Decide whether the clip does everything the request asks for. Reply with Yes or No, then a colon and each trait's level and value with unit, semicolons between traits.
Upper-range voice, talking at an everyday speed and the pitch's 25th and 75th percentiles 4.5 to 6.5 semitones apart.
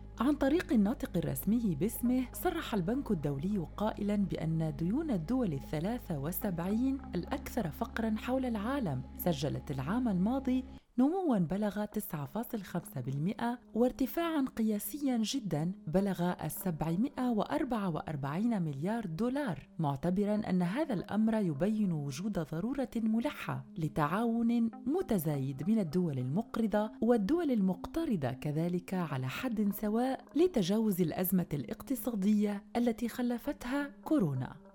Yes: high, 210 Hz; average, 95 wpm; wide, 5.6 semitones